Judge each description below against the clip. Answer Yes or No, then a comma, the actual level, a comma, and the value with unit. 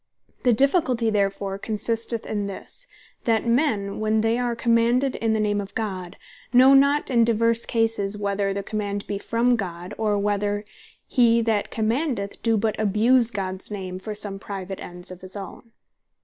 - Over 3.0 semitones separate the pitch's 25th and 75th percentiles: No, narrow, 2.6 semitones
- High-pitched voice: Yes, high, 215 Hz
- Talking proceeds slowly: No, average, 165 wpm